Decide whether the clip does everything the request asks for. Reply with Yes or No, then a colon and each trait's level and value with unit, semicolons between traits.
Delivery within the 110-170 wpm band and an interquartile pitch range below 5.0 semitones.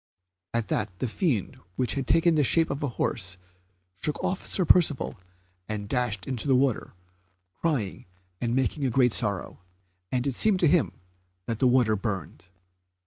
No: average, 160 wpm; average, 5.3 semitones